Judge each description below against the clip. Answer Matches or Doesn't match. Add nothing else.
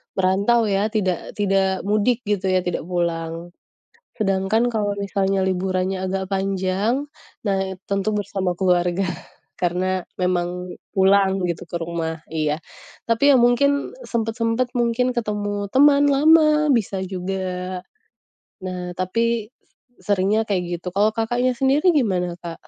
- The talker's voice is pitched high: Matches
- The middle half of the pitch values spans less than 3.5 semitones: Doesn't match